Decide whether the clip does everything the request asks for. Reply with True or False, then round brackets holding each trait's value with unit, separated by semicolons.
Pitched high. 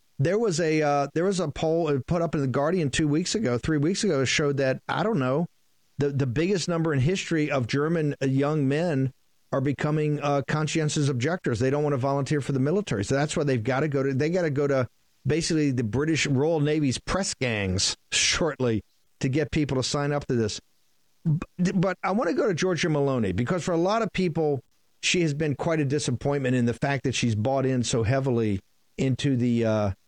False (145 Hz)